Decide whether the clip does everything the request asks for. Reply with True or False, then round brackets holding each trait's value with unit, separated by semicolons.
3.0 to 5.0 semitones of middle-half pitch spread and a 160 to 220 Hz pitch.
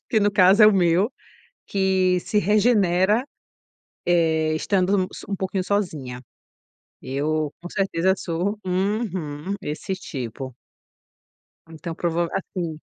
True (3.6 semitones; 185 Hz)